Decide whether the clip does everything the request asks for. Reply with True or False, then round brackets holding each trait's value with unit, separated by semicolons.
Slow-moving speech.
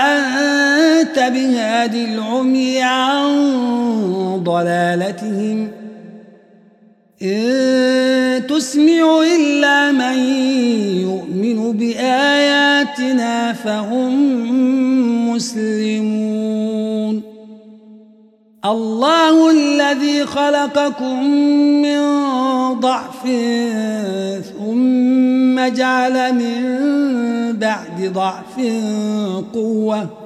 True (45 wpm)